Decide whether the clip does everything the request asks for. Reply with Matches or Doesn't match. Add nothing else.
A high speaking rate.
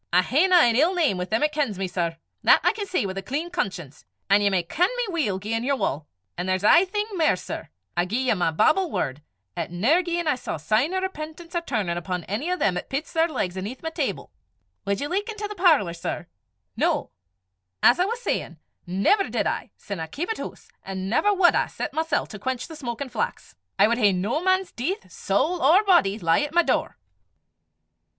Matches